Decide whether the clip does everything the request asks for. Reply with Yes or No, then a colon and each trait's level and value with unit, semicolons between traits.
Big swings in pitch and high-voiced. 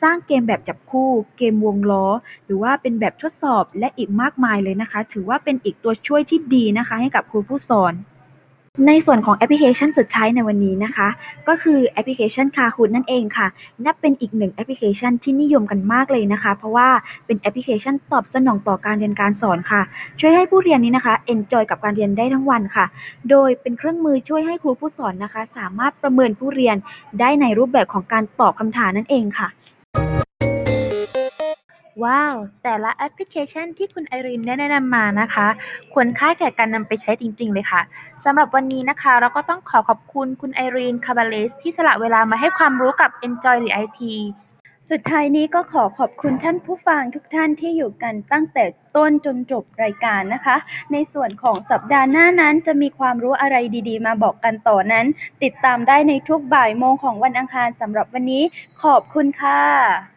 No: average, 4.6 semitones; very high, 250 Hz